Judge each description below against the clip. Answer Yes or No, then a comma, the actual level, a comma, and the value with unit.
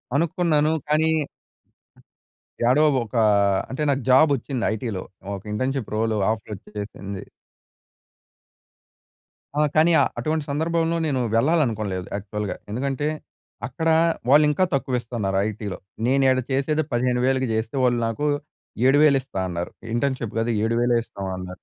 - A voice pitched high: No, low, 130 Hz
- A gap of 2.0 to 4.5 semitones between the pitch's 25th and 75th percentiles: No, average, 5.2 semitones